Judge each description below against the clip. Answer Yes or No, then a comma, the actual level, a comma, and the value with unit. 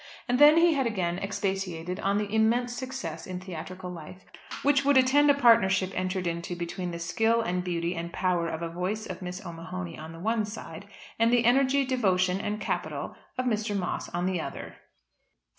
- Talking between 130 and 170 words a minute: No, average, 185 wpm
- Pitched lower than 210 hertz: Yes, high, 190 Hz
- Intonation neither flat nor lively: Yes, average, 4.8 semitones